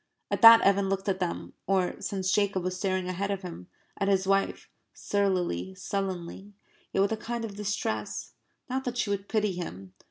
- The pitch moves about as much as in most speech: No, narrow, 1.8 semitones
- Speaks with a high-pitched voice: Yes, high, 195 Hz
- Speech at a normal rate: Yes, average, 185 wpm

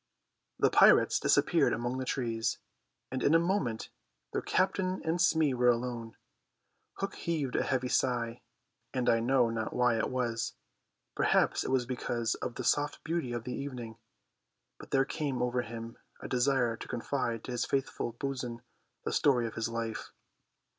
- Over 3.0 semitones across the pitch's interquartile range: No, average, 2.7 semitones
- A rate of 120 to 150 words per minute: No, average, 165 wpm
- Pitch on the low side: Yes, low, 125 Hz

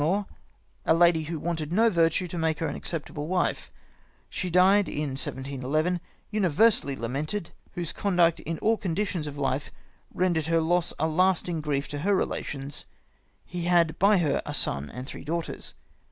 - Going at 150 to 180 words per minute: Yes, average, 170 wpm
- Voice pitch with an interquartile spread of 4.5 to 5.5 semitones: No, average, 3.4 semitones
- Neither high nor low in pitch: Yes, medium, 165 Hz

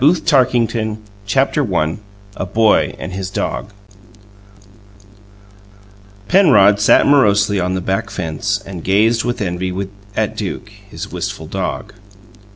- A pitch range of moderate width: Yes, average, 4.2 semitones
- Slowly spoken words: Yes, slow, 125 wpm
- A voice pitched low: Yes, low, 105 Hz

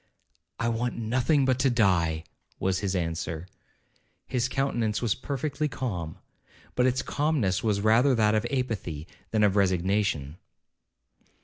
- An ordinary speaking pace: No, slow, 130 wpm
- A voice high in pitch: No, low, 110 Hz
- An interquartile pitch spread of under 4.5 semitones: No, wide, 5.4 semitones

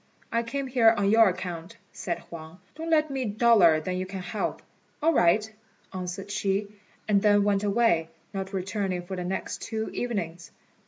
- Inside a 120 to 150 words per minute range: No, average, 175 wpm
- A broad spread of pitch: No, average, 3.8 semitones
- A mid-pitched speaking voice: No, high, 200 Hz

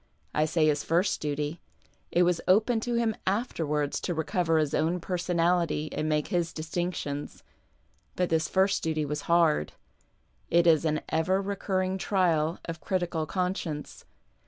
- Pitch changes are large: No, average, 2.9 semitones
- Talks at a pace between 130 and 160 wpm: Yes, average, 145 wpm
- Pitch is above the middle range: No, medium, 170 Hz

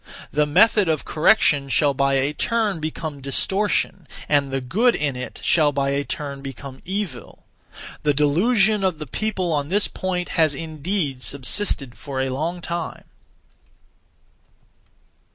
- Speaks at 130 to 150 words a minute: Yes, average, 140 wpm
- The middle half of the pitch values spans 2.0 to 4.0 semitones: No, average, 5.1 semitones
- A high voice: No, medium, 150 Hz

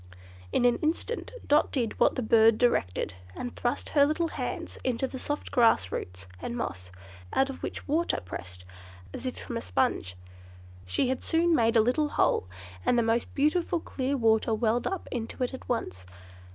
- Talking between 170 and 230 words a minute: Yes, average, 180 wpm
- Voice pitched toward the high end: Yes, high, 245 Hz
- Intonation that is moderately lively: Yes, average, 4.1 semitones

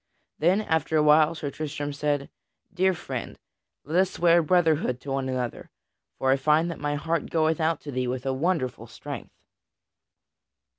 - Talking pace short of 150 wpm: No, average, 165 wpm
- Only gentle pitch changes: No, average, 3.3 semitones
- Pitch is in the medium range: Yes, medium, 150 Hz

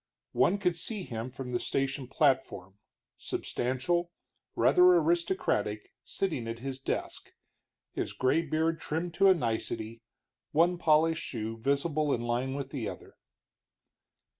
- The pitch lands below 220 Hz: Yes, medium, 140 Hz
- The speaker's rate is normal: No, slow, 130 wpm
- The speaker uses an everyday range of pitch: No, wide, 5.8 semitones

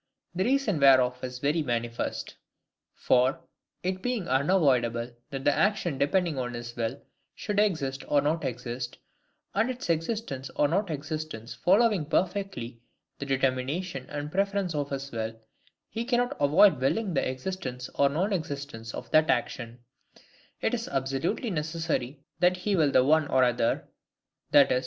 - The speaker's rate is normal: Yes, average, 150 wpm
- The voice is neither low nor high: Yes, medium, 145 Hz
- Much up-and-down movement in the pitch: Yes, wide, 6.2 semitones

